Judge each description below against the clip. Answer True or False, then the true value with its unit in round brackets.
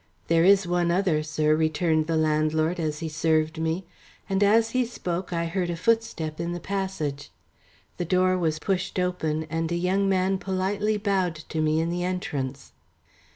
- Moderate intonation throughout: True (3.2 semitones)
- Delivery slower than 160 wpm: False (175 wpm)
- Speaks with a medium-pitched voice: True (170 Hz)